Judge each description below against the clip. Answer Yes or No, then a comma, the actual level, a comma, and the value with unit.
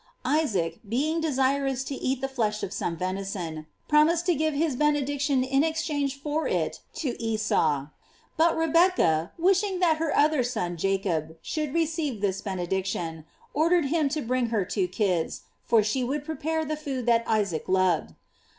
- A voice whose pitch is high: Yes, very high, 265 Hz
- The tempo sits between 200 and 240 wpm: No, average, 165 wpm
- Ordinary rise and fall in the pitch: No, wide, 8.0 semitones